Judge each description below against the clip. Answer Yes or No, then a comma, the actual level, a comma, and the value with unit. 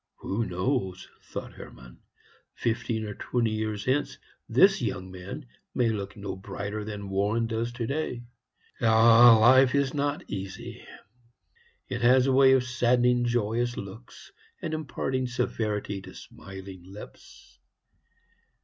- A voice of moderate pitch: No, low, 115 Hz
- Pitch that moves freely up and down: No, average, 3.8 semitones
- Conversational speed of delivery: No, slow, 125 wpm